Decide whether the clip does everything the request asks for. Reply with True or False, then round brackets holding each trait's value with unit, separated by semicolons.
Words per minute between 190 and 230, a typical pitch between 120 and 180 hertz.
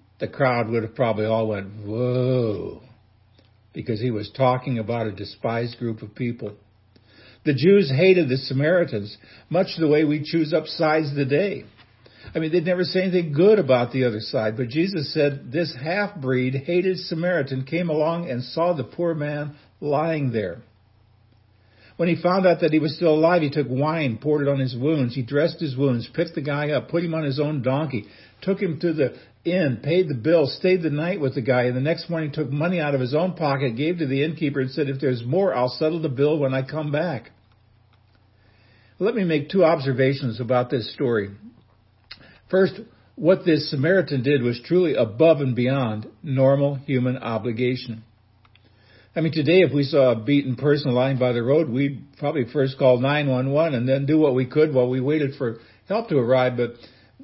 True (195 wpm; 135 Hz)